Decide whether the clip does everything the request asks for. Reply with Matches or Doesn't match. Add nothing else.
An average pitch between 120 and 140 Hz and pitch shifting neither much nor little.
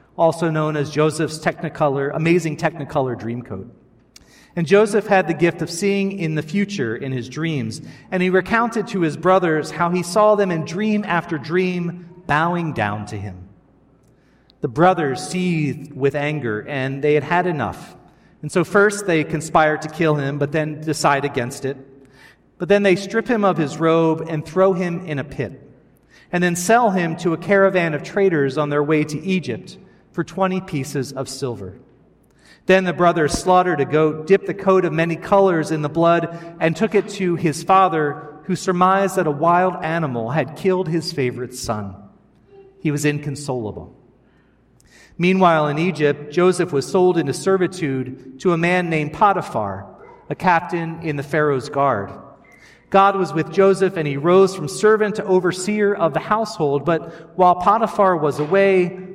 Doesn't match